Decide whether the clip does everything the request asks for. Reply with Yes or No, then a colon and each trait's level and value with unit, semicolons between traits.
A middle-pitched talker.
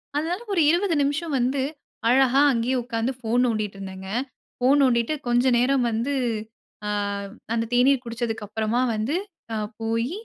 No: high, 245 Hz